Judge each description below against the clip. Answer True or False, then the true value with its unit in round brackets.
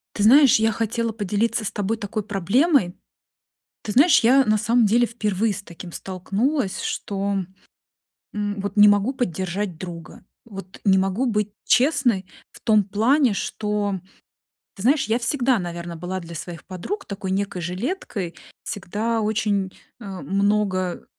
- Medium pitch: False (205 Hz)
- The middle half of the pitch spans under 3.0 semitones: False (3.4 semitones)